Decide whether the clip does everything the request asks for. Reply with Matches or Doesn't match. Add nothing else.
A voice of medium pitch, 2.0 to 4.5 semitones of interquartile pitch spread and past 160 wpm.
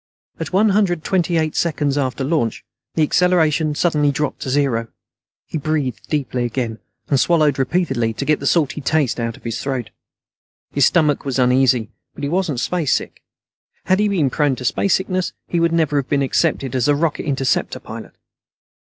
Matches